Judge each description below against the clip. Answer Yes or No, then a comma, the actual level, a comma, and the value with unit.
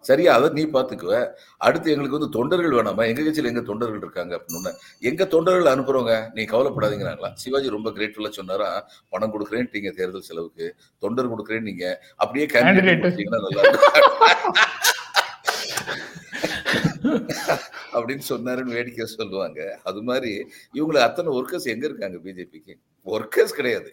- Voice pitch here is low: Yes, low, 130 Hz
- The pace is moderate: Yes, average, 120 wpm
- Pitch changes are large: Yes, wide, 8.8 semitones